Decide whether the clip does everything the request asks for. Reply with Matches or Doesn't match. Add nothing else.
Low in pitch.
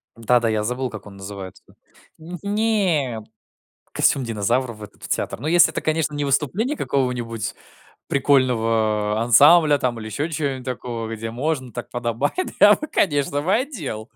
Matches